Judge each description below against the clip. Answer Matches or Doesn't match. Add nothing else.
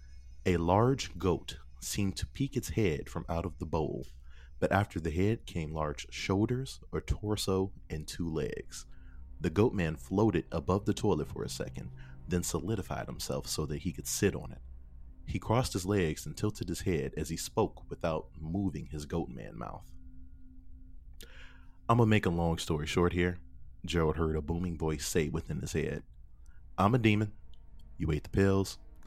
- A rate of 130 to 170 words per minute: Doesn't match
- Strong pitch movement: Matches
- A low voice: Matches